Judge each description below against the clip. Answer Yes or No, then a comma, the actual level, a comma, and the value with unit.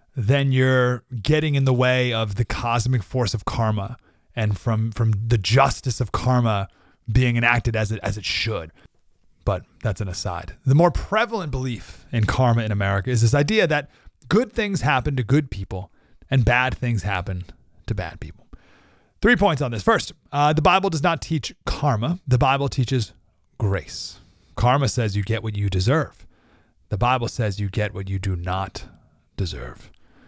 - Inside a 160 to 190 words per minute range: Yes, average, 175 wpm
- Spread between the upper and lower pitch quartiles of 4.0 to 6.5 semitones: Yes, average, 4.5 semitones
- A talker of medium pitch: No, low, 115 Hz